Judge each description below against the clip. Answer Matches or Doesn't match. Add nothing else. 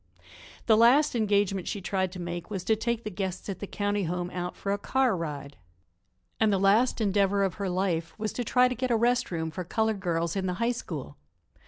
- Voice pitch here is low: Doesn't match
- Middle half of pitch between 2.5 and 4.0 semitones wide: Matches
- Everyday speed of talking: Doesn't match